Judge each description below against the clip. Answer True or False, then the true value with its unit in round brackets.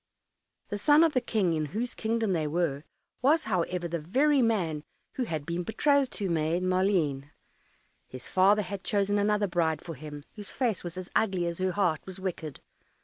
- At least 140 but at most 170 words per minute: False (185 wpm)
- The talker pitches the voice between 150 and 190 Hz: True (185 Hz)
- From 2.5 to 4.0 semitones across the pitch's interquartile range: False (4.5 semitones)